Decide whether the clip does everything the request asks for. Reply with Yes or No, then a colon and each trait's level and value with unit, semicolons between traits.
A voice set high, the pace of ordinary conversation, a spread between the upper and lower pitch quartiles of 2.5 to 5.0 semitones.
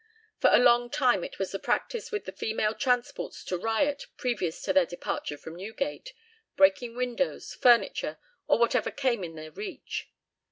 No: high, 240 Hz; average, 165 wpm; wide, 5.6 semitones